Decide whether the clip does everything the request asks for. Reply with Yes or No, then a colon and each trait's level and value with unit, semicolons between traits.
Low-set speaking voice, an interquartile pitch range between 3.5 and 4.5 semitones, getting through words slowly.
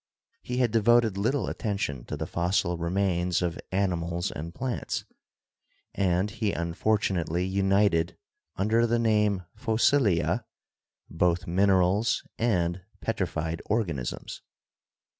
Yes: very low, 95 Hz; average, 4.2 semitones; slow, 105 wpm